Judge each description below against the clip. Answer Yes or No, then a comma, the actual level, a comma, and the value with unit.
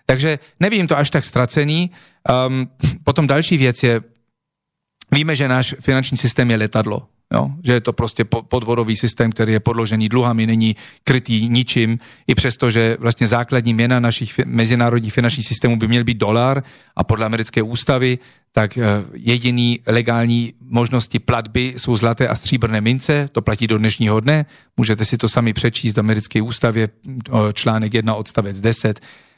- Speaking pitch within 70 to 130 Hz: Yes, low, 120 Hz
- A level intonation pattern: Yes, narrow, 2.2 semitones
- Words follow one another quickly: No, average, 155 wpm